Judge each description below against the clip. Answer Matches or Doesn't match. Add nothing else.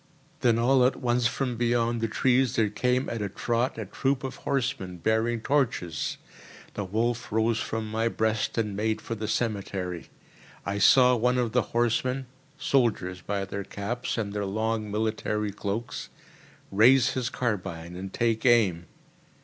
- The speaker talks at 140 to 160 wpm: Matches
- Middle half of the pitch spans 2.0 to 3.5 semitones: Matches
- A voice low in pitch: Matches